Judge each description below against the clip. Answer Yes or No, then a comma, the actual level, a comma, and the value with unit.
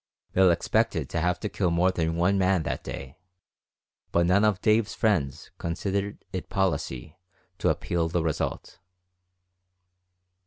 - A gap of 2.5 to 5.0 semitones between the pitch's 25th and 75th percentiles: Yes, average, 2.9 semitones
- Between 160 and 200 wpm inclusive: No, average, 140 wpm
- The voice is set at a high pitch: No, very low, 90 Hz